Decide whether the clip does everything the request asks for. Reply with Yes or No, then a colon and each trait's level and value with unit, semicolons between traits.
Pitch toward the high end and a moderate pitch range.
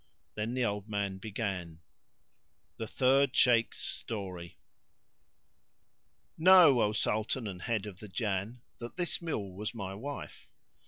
No: low, 110 Hz; average, 4.0 semitones